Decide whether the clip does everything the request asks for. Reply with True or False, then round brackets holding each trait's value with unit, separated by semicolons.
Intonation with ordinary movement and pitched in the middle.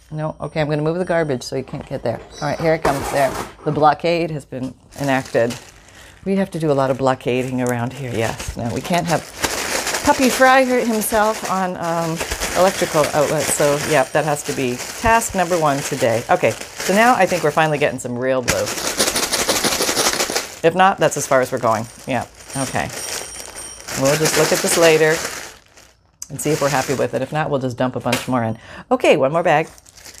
True (4.8 semitones; 145 Hz)